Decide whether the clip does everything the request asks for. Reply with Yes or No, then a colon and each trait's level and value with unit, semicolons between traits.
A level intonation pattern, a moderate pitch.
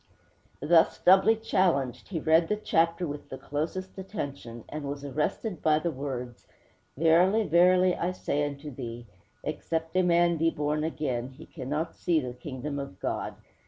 No: average, 3.8 semitones; medium, 155 Hz